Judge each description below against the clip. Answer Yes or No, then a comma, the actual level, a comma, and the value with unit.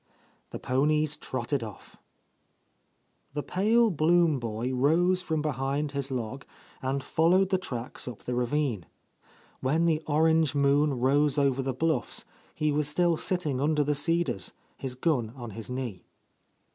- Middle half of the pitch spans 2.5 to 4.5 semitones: Yes, average, 3.7 semitones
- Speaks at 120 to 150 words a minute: Yes, average, 145 wpm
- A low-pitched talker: No, medium, 145 Hz